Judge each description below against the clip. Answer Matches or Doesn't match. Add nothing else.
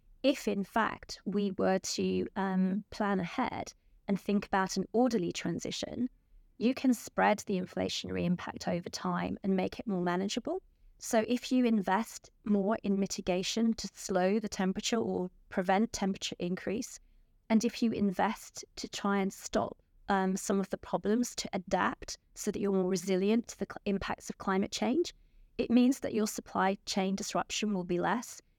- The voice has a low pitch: Doesn't match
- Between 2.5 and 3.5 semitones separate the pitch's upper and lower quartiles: Matches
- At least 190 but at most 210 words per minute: Doesn't match